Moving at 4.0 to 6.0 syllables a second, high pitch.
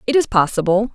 No: 6.3 syllables/s; high, 210 Hz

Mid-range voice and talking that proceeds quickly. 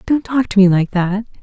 No: high, 210 Hz; fast, 250 wpm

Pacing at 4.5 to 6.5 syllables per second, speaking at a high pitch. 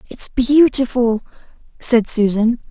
No: 3.6 syllables/s; high, 240 Hz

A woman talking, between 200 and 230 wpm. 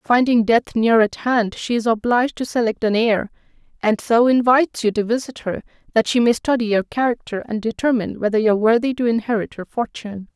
Yes: female; fast, 205 wpm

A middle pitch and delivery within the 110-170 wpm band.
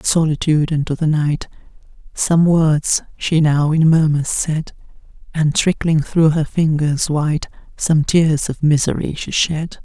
Yes: medium, 155 Hz; average, 150 wpm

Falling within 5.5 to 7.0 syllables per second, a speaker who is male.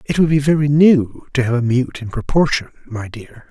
No: 5.1 syllables/s; male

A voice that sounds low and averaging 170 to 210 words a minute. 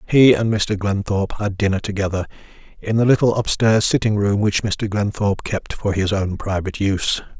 Yes: low, 105 Hz; average, 180 wpm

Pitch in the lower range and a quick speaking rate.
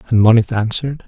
No: low, 115 Hz; average, 170 wpm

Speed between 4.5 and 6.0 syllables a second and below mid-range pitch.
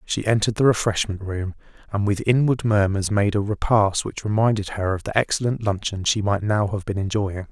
Yes: 5.4 syllables/s; low, 105 Hz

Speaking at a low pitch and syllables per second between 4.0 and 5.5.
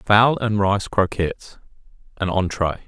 Yes: low, 100 Hz; 4.2 syllables/s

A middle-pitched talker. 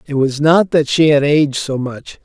Yes: medium, 145 Hz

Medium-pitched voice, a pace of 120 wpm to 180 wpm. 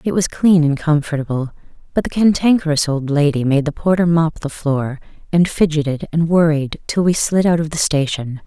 No: medium, 155 Hz; average, 190 wpm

